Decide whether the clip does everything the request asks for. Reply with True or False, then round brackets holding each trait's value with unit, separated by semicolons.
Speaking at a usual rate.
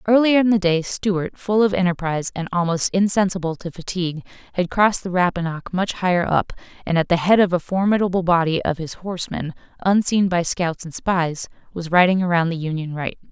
True (190 wpm)